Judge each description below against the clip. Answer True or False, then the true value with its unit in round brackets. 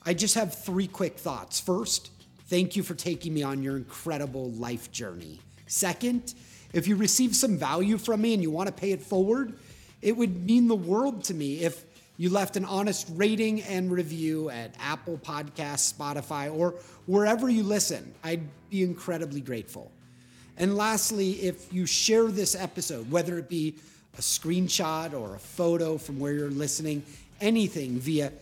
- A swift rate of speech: False (170 wpm)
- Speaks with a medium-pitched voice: True (175 Hz)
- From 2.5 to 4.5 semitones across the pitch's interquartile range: False (5.3 semitones)